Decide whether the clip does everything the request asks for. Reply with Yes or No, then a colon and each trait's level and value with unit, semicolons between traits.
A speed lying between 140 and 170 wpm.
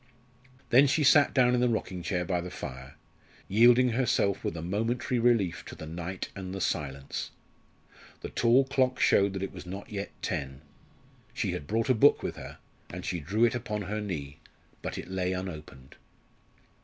No: average, 180 wpm